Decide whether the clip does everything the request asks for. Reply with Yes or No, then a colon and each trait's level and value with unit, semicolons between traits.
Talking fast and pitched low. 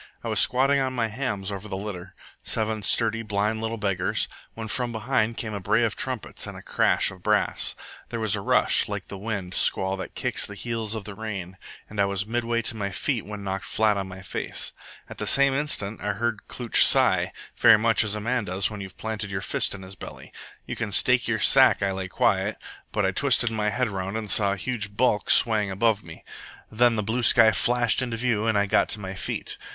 Yes: fast, 225 wpm; low, 105 Hz